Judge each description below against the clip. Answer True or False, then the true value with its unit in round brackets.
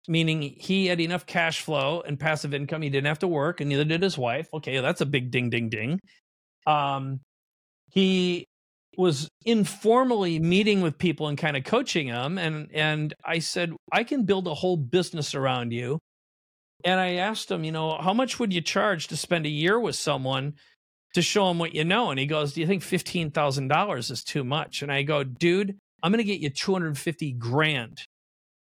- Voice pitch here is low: False (160 Hz)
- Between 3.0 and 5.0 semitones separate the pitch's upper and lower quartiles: True (4.1 semitones)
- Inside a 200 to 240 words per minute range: True (205 wpm)